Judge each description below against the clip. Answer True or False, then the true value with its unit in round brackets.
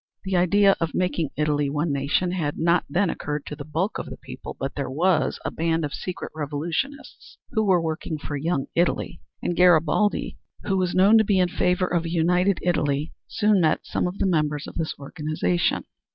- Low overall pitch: False (165 Hz)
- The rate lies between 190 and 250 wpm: True (195 wpm)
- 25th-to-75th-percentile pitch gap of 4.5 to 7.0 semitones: False (3.5 semitones)